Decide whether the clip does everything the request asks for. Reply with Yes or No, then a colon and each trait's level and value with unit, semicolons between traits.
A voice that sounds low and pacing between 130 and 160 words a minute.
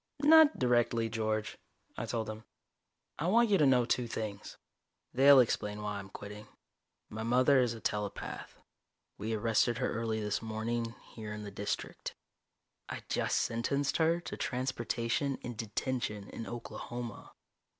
Yes: low, 115 Hz; average, 145 wpm